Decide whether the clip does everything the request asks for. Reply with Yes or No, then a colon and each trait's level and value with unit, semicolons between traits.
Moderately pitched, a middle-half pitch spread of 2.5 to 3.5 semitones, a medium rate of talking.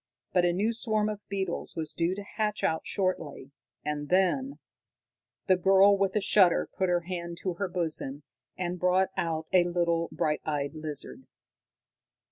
Yes: medium, 180 Hz; average, 2.9 semitones; average, 160 wpm